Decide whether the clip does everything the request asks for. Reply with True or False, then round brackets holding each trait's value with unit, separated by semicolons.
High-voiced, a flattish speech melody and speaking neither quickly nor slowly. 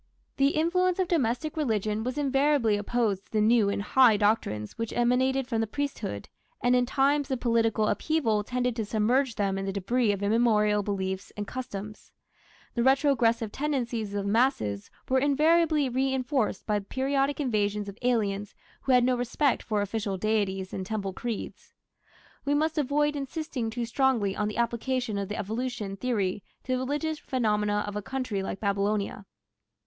False (235 Hz; 4.4 semitones; 170 wpm)